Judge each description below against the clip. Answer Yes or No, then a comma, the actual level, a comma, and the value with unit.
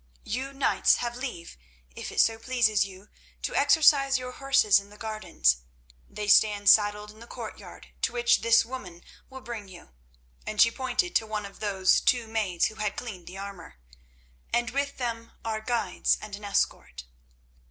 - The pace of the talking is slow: No, average, 175 wpm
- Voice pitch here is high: Yes, high, 220 Hz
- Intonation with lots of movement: No, average, 3.8 semitones